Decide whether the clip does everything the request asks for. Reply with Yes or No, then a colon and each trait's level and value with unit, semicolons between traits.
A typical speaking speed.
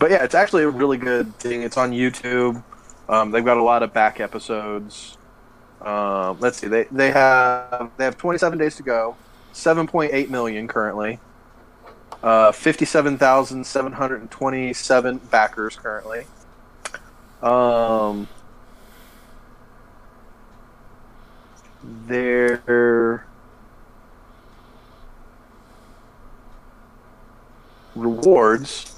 No: slow, 105 wpm